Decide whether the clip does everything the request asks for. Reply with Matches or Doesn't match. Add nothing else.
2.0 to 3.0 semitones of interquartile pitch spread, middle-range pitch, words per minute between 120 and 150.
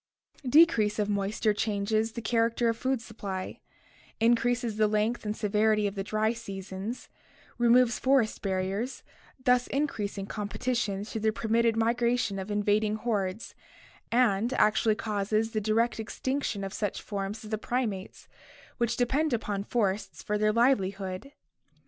Doesn't match